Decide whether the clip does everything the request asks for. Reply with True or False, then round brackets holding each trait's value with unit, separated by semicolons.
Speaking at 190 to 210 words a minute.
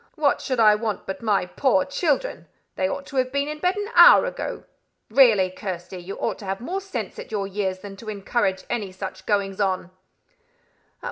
True (195 wpm)